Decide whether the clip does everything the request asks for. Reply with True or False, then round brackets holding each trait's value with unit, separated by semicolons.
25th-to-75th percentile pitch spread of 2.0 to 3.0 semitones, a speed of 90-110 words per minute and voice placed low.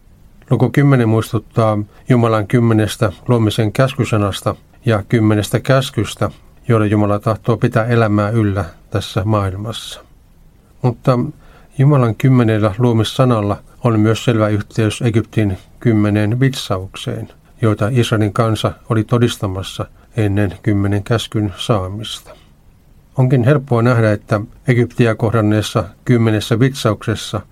True (2.5 semitones; 100 wpm; 110 Hz)